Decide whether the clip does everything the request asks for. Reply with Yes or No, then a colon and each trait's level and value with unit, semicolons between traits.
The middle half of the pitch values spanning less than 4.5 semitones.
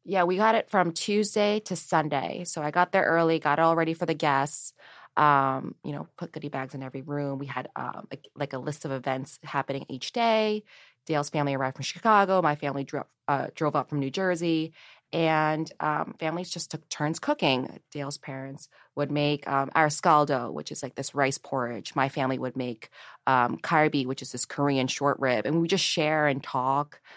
Yes: average, 3.3 semitones